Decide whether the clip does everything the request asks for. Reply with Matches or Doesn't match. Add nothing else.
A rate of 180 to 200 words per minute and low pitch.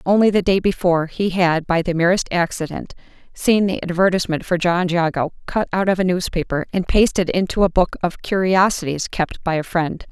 Doesn't match